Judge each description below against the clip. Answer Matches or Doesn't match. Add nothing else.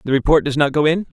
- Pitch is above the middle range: Doesn't match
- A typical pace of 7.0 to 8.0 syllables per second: Matches